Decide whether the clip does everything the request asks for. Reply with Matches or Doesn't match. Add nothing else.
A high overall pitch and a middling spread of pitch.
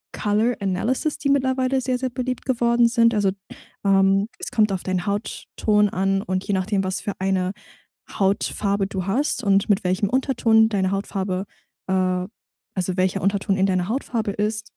Matches